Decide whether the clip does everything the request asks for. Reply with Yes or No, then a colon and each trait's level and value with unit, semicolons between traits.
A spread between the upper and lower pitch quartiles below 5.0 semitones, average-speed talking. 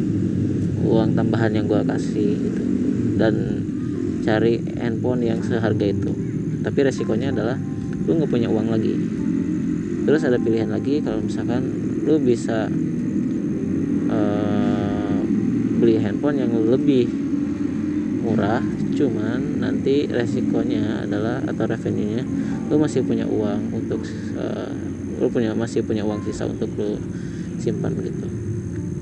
No: average, 5.3 semitones; average, 120 wpm